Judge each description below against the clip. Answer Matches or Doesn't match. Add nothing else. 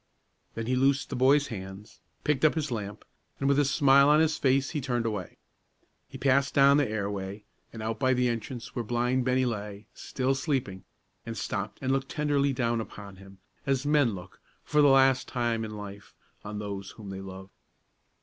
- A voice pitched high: Doesn't match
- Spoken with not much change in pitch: Doesn't match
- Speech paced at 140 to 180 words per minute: Doesn't match